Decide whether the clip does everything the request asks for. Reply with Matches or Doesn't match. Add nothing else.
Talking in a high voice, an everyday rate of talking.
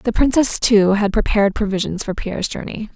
Matches